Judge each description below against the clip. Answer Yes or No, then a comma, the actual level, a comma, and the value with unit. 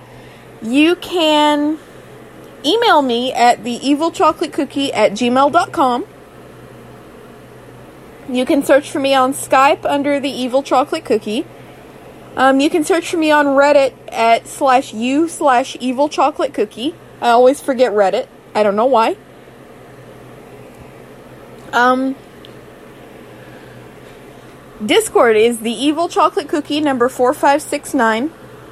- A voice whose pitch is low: No, very high, 275 Hz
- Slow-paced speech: Yes, slow, 110 wpm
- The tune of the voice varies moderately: Yes, average, 3.7 semitones